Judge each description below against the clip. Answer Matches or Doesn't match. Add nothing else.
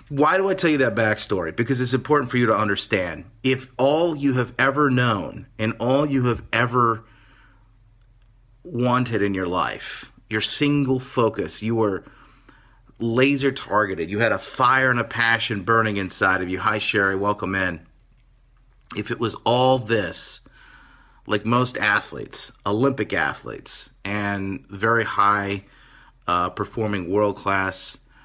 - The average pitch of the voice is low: Matches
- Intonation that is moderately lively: Matches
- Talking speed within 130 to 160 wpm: Matches